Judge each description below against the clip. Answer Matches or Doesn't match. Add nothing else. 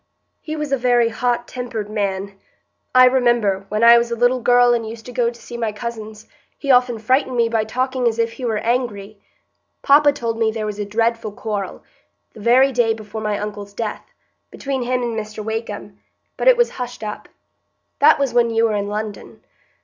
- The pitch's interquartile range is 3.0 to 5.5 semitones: Doesn't match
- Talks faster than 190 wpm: Matches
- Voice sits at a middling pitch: Doesn't match